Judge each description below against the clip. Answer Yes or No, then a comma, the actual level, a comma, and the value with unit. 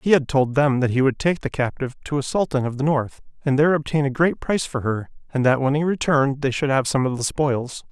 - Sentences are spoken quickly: Yes, fast, 275 wpm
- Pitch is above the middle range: No, medium, 140 Hz